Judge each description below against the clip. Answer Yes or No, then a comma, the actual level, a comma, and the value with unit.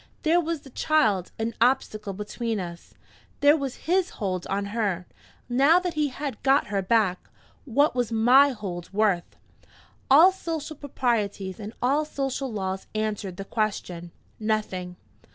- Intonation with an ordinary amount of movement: No, wide, 6.1 semitones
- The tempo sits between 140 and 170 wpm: Yes, average, 145 wpm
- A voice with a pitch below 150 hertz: No, high, 225 Hz